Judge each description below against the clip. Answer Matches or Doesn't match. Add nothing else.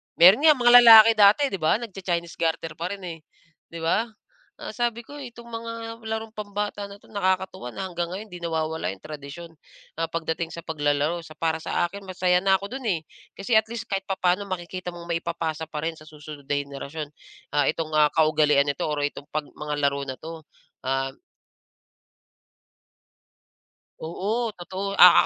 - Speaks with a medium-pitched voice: Matches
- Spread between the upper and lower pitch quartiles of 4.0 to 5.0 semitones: Matches